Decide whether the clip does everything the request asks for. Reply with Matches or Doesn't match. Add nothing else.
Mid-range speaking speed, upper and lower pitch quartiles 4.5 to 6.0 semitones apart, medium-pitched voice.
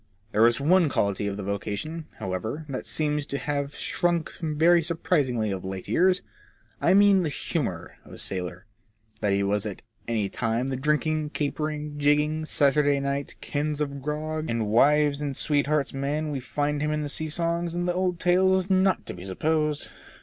Matches